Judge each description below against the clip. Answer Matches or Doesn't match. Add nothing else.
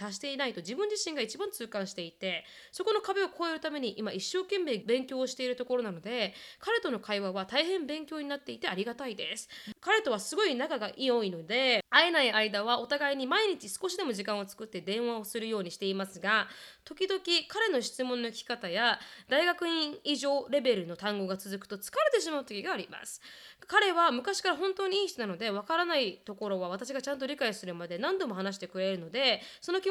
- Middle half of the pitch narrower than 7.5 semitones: Doesn't match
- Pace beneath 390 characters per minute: Doesn't match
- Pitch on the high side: Matches